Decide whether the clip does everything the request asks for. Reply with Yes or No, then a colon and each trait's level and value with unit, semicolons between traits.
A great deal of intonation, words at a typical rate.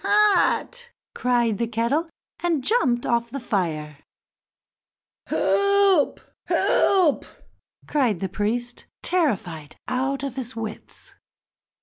No: wide, 7.1 semitones; slow, 95 wpm